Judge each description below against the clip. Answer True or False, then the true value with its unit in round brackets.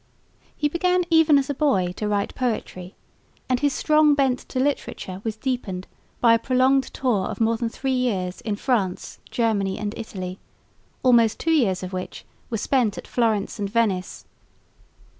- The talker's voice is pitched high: True (230 Hz)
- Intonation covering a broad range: False (5.0 semitones)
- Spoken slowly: False (165 wpm)